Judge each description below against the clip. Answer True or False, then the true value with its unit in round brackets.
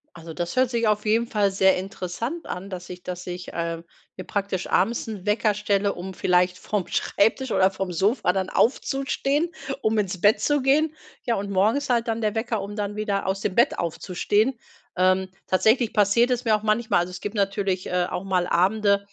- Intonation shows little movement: False (3.4 semitones)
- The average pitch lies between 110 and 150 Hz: False (200 Hz)